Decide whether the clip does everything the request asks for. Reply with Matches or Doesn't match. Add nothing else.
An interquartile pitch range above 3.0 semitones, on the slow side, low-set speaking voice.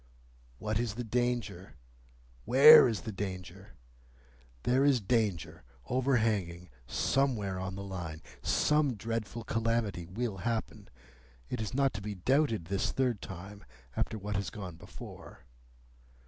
Matches